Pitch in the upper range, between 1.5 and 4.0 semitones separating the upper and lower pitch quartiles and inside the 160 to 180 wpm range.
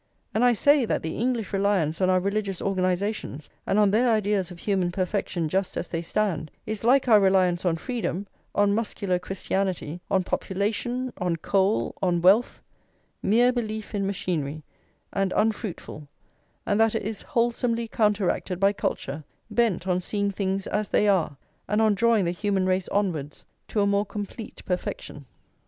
Yes: high, 200 Hz; average, 3.0 semitones; average, 165 wpm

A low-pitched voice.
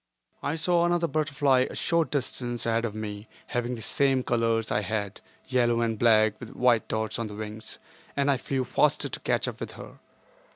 Yes: low, 120 Hz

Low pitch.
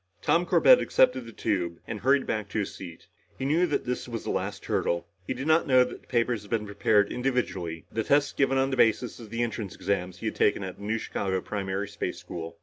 Yes: low, 110 Hz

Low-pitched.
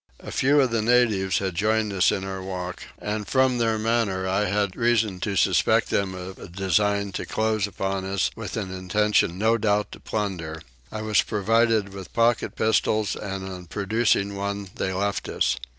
Yes: low, 100 Hz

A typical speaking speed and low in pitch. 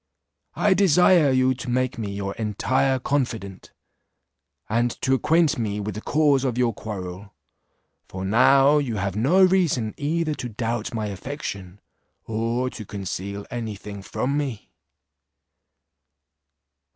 No: slow, 130 wpm; low, 120 Hz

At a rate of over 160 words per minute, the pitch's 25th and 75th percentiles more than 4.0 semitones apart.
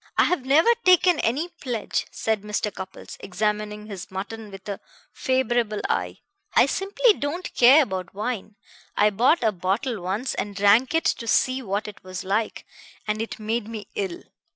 Yes: average, 170 wpm; average, 4.4 semitones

